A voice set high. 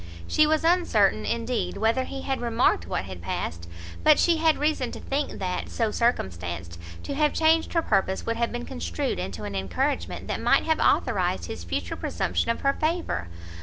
Yes: high, 230 Hz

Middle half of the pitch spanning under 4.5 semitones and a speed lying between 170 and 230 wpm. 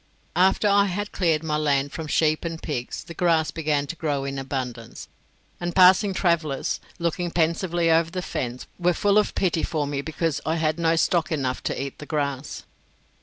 Yes: average, 3.3 semitones; average, 185 wpm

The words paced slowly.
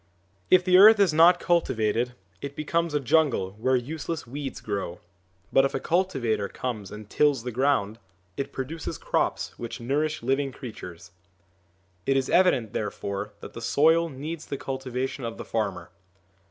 No: average, 155 wpm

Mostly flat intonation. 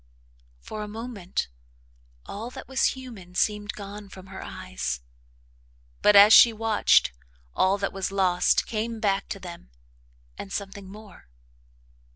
Yes: narrow, 2.2 semitones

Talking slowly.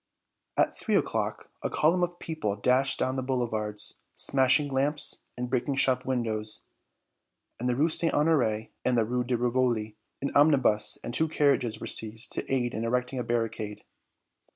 No: average, 170 wpm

